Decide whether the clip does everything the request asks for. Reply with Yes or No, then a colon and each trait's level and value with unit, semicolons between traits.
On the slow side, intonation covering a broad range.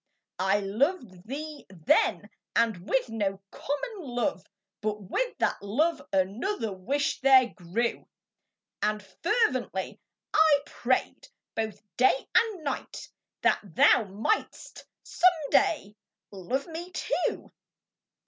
Yes: slow, 110 wpm; wide, 7.5 semitones